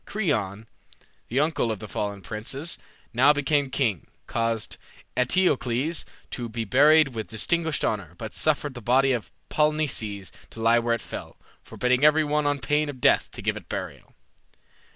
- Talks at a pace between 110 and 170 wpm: Yes, average, 160 wpm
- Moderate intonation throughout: Yes, average, 4.9 semitones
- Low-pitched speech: Yes, low, 125 Hz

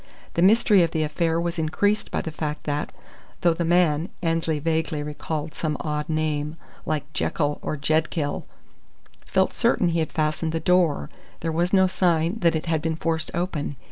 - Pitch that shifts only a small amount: Yes, narrow, 2.0 semitones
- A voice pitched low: No, medium, 160 Hz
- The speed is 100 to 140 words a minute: No, average, 175 wpm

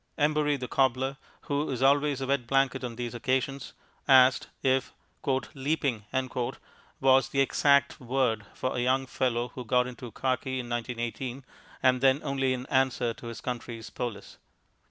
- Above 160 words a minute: No, average, 155 wpm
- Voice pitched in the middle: No, low, 130 Hz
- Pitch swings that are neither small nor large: No, narrow, 1.7 semitones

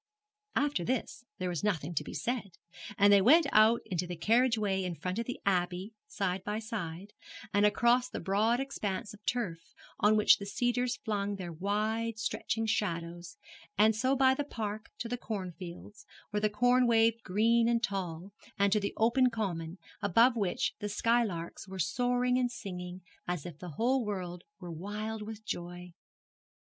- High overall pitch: Yes, high, 210 Hz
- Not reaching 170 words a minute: No, average, 175 wpm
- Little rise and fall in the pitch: No, average, 4.2 semitones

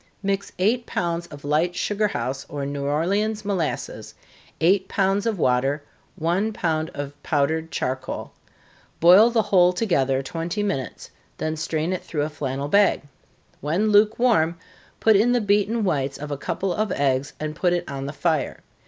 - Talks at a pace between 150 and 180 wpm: Yes, average, 165 wpm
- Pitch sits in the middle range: Yes, medium, 170 Hz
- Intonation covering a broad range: Yes, wide, 5.9 semitones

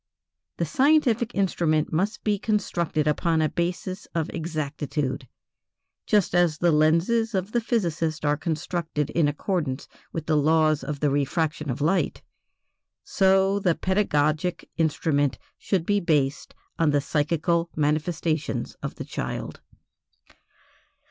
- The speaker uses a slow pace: Yes, slow, 125 wpm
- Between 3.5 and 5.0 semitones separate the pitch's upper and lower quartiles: Yes, average, 3.8 semitones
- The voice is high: No, medium, 165 Hz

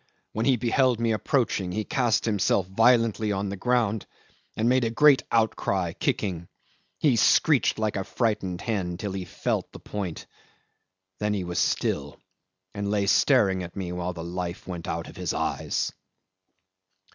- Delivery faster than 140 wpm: Yes, average, 160 wpm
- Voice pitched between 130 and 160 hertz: No, low, 105 Hz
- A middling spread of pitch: Yes, average, 3.9 semitones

